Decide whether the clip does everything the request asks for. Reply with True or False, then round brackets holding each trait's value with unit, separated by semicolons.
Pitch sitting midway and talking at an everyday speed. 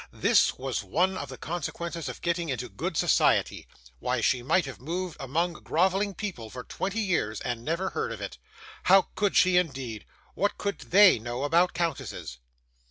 True (165 Hz; 170 wpm)